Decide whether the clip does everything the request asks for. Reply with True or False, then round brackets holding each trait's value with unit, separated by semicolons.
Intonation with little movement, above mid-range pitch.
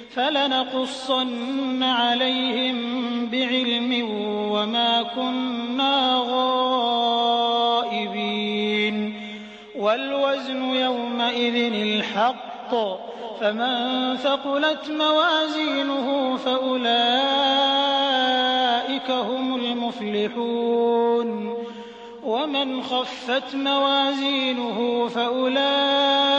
True (2.1 semitones; 250 Hz)